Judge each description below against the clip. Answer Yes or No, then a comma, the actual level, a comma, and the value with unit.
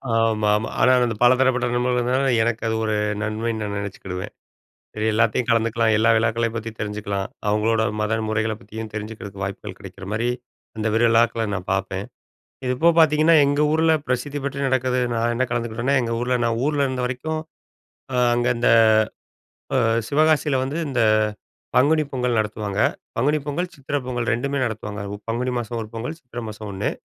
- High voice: No, low, 115 Hz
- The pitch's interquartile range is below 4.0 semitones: Yes, average, 3.0 semitones